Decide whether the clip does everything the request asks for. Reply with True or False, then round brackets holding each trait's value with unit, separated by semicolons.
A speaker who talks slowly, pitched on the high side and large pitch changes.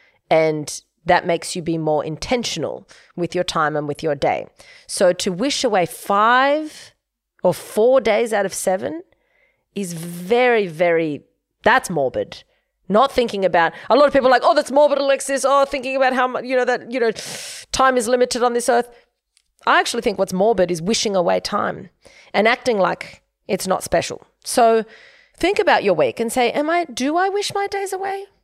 False (185 wpm; 245 Hz; 7.5 semitones)